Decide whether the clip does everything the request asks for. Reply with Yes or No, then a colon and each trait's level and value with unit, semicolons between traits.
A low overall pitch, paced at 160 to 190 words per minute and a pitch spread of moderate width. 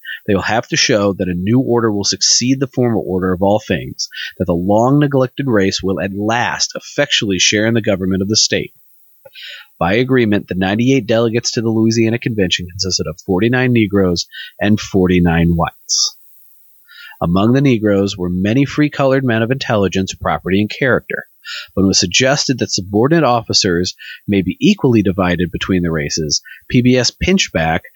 Yes: low, 105 Hz; average, 175 wpm; average, 5.0 semitones